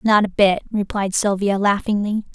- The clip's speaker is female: Yes, female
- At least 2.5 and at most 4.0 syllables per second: No, 4.8 syllables/s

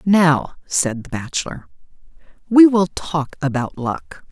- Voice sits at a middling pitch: Yes, medium, 160 Hz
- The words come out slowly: Yes, slow, 125 wpm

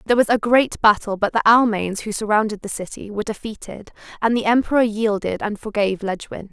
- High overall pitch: Yes, high, 215 Hz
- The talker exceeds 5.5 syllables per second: Yes, 5.9 syllables/s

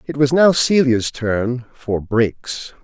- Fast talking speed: No, average, 150 wpm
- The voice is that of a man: Yes, male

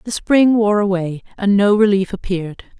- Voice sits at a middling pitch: No, high, 200 Hz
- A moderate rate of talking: Yes, average, 170 wpm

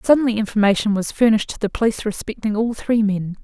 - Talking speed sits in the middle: Yes, average, 190 wpm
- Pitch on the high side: Yes, high, 215 Hz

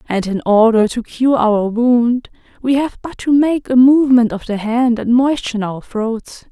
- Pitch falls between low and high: No, high, 240 Hz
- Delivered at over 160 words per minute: Yes, average, 195 wpm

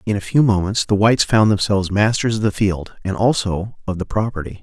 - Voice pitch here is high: No, low, 100 Hz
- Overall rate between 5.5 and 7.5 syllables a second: Yes, 5.8 syllables/s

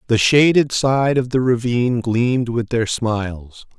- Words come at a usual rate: Yes, average, 160 wpm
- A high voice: No, low, 120 Hz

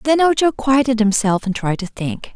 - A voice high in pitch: Yes, high, 235 Hz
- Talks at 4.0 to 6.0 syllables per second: Yes, 4.9 syllables/s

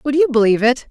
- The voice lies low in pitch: No, very high, 255 Hz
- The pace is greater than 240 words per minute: Yes, fast, 265 wpm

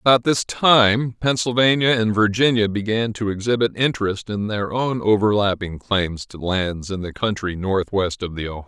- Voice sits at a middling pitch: No, low, 105 Hz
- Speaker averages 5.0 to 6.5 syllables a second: No, 4.8 syllables/s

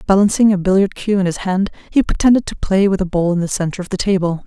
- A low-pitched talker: No, high, 190 Hz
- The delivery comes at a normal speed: No, fast, 270 wpm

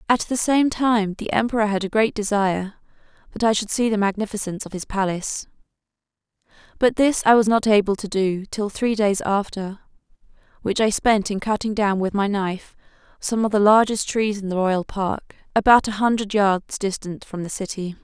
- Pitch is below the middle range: No, high, 205 Hz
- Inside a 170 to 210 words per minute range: Yes, average, 190 wpm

